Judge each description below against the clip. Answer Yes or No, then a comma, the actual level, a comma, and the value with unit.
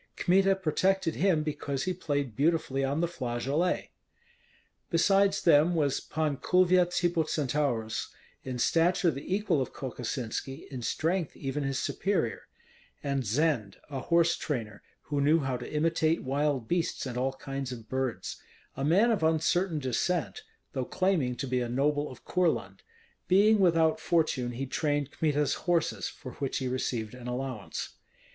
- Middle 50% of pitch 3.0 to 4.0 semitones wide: No, average, 4.6 semitones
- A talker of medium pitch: Yes, medium, 145 Hz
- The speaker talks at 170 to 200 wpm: No, average, 150 wpm